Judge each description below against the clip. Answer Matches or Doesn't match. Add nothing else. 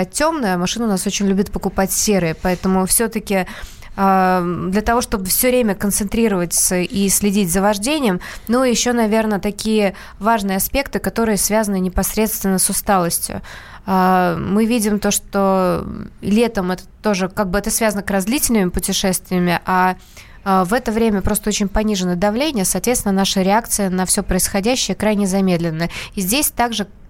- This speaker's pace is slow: Doesn't match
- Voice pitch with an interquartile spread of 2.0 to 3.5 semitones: Matches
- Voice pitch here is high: Matches